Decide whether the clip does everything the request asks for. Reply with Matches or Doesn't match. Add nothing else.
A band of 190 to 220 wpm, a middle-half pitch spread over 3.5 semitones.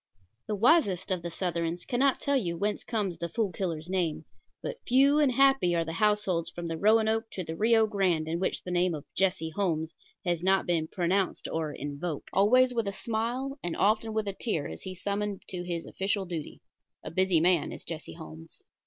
Matches